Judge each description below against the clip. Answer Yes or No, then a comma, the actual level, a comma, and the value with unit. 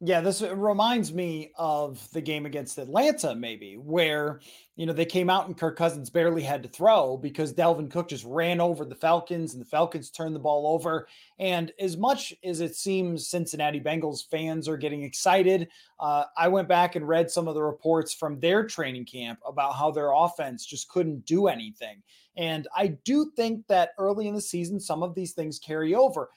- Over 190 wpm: Yes, average, 200 wpm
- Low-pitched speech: No, medium, 165 Hz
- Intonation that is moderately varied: Yes, average, 3.3 semitones